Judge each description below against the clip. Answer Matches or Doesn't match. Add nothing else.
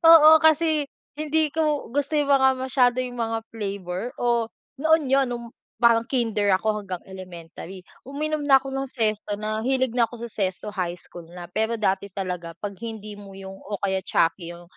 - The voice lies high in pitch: Matches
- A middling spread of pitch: Doesn't match